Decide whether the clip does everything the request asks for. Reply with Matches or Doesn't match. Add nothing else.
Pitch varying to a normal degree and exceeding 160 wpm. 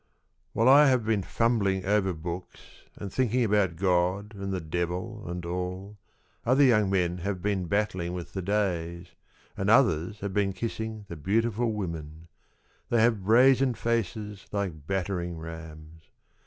Doesn't match